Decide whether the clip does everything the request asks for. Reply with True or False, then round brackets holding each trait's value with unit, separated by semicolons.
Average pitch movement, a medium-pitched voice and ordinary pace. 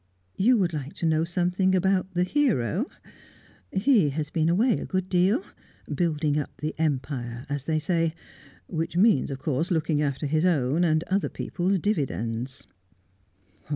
True (4.2 semitones; 165 Hz; 155 wpm)